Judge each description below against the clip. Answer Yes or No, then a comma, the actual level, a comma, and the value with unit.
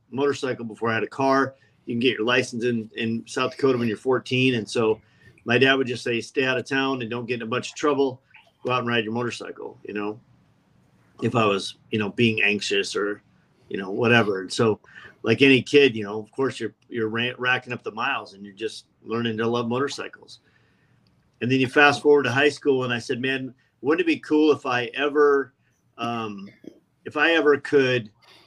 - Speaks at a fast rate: Yes, fast, 215 wpm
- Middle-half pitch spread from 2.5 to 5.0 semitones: Yes, average, 2.9 semitones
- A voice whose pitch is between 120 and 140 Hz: Yes, low, 125 Hz